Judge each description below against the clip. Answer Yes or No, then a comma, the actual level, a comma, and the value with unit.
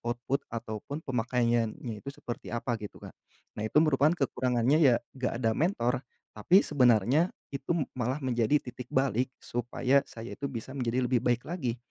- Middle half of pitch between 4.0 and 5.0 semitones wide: No, average, 2.8 semitones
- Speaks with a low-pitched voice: Yes, low, 125 Hz